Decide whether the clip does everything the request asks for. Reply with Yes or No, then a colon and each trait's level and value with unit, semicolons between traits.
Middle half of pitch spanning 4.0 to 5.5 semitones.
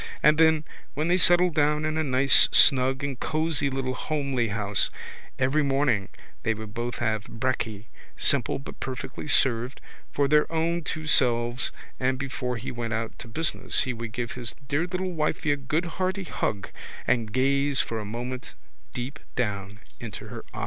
Yes: average, 4.5 semitones